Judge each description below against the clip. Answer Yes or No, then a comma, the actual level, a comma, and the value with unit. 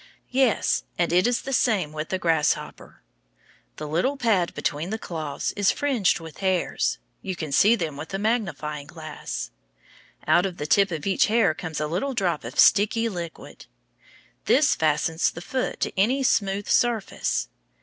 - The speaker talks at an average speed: Yes, average, 170 wpm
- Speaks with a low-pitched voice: No, medium, 185 Hz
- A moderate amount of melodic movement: No, wide, 5.9 semitones